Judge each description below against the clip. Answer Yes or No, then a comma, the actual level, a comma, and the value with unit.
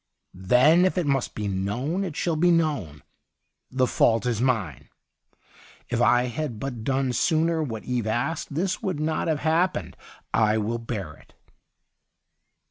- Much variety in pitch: Yes, wide, 6.0 semitones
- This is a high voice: No, low, 130 Hz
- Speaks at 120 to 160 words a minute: Yes, average, 155 wpm